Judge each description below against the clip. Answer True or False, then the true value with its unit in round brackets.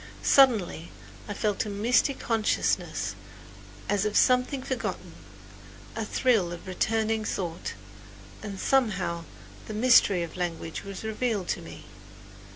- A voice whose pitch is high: True (210 Hz)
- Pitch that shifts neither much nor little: True (4.1 semitones)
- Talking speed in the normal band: False (120 wpm)